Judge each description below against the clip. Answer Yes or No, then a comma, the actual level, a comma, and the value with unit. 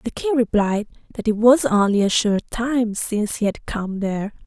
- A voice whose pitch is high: Yes, high, 220 Hz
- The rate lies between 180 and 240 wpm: Yes, average, 200 wpm